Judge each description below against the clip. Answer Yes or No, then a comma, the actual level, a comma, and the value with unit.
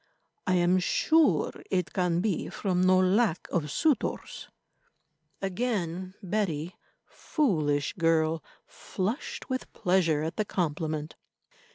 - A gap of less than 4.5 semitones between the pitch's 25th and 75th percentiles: Yes, average, 3.6 semitones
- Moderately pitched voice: Yes, medium, 180 Hz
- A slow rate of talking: Yes, slow, 105 wpm